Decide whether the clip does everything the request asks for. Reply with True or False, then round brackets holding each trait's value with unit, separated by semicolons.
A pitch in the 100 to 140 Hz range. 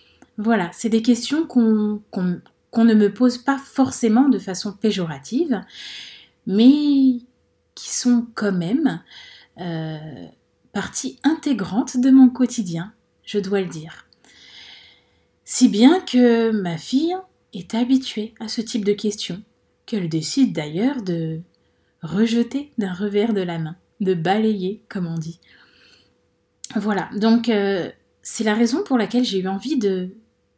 False (220 Hz)